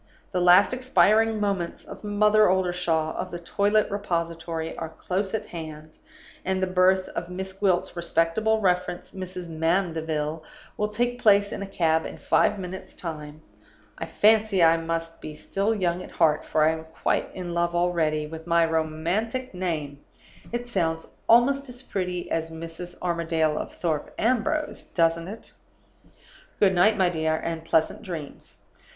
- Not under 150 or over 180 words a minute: Yes, average, 155 wpm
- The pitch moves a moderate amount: Yes, average, 3.6 semitones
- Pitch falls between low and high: Yes, medium, 175 Hz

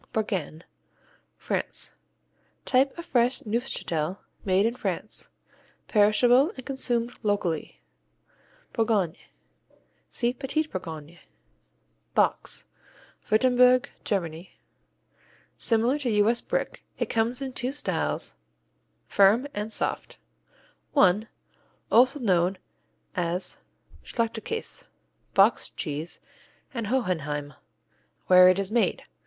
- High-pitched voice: Yes, high, 220 Hz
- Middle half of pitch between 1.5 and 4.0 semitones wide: No, average, 5.3 semitones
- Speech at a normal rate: No, slow, 90 wpm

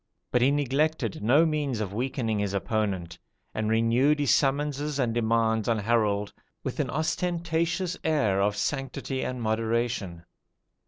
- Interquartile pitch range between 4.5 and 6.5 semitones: Yes, average, 5.1 semitones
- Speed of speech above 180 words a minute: No, average, 140 wpm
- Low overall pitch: Yes, low, 120 Hz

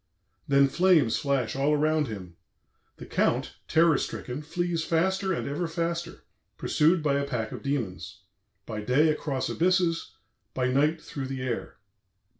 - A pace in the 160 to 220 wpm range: No, average, 145 wpm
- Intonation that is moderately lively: Yes, average, 4.3 semitones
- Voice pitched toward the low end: No, medium, 150 Hz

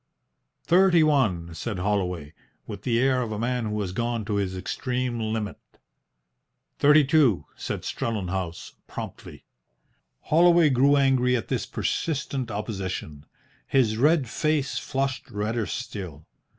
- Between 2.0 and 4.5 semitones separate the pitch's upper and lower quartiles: No, wide, 5.5 semitones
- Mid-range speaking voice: No, low, 115 Hz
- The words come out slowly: Yes, slow, 125 wpm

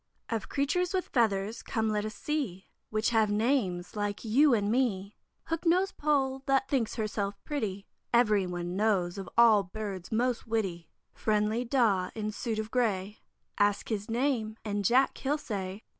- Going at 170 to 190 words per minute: No, average, 160 wpm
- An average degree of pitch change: Yes, average, 3.8 semitones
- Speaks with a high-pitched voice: Yes, high, 220 Hz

